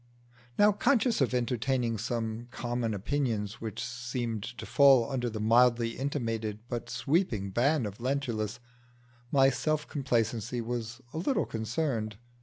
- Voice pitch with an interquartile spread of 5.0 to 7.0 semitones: No, average, 3.1 semitones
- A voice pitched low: Yes, low, 120 Hz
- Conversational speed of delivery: No, slow, 130 wpm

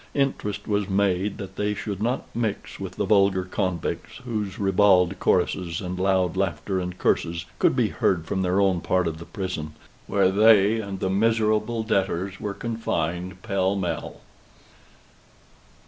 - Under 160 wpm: Yes, average, 150 wpm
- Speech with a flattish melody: Yes, narrow, 2.3 semitones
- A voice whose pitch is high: No, very low, 95 Hz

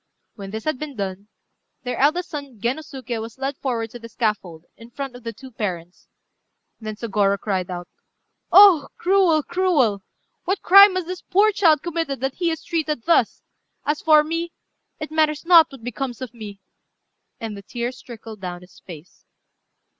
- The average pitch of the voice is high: Yes, very high, 260 Hz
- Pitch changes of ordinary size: No, wide, 6.7 semitones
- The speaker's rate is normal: Yes, average, 170 wpm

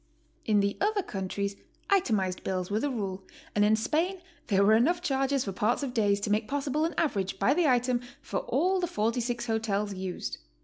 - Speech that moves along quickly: No, average, 190 wpm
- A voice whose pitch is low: No, high, 225 Hz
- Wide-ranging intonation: Yes, wide, 5.8 semitones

